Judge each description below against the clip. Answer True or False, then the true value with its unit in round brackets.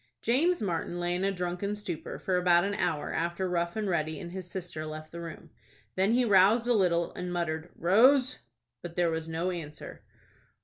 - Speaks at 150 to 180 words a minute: False (190 wpm)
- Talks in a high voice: False (175 Hz)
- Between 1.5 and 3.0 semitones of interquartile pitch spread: True (2.7 semitones)